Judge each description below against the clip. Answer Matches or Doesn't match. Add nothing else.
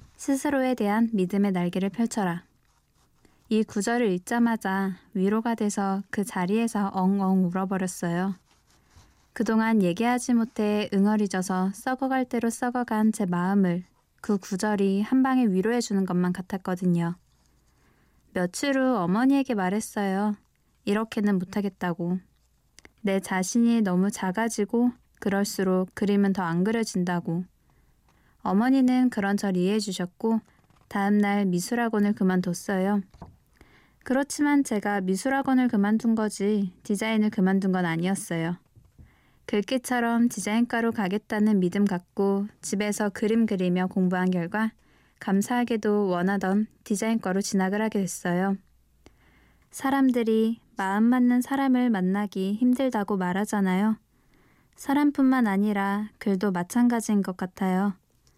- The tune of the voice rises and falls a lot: Doesn't match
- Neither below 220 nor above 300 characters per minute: Matches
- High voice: Matches